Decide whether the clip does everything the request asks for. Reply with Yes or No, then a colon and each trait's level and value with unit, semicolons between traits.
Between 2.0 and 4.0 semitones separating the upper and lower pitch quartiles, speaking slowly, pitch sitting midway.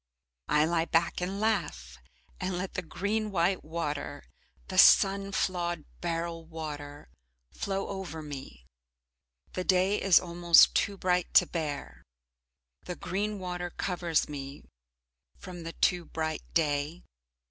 Yes: average, 3.2 semitones; slow, 125 wpm; medium, 170 Hz